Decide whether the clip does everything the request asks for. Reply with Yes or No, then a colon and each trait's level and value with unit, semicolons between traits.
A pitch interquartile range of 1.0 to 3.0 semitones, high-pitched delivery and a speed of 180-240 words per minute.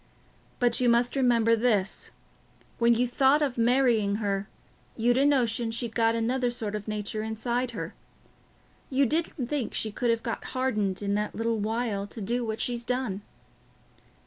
No: narrow, 2.4 semitones; high, 235 Hz; average, 170 wpm